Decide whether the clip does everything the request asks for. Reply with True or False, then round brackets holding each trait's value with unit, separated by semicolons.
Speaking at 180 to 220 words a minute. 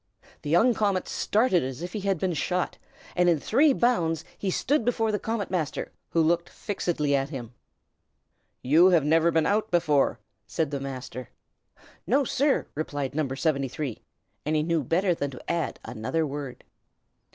False (165 wpm)